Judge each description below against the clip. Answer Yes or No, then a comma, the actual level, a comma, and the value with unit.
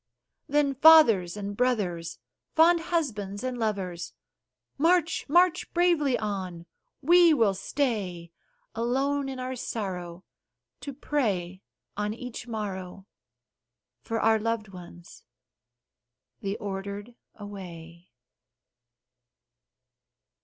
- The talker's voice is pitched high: Yes, high, 215 Hz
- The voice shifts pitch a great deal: Yes, wide, 6.5 semitones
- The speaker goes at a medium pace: No, slow, 90 wpm